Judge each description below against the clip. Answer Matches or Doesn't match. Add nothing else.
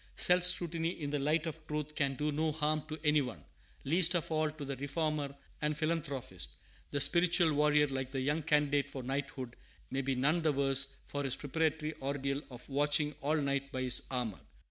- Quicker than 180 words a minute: Matches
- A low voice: Doesn't match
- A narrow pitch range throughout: Matches